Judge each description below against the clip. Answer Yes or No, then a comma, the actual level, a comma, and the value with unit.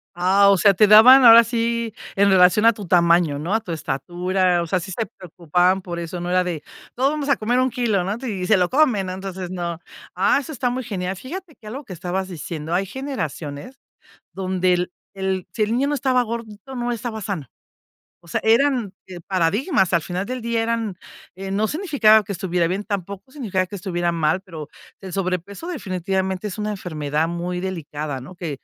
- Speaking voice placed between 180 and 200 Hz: Yes, high, 190 Hz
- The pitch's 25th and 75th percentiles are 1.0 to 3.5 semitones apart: No, average, 4.4 semitones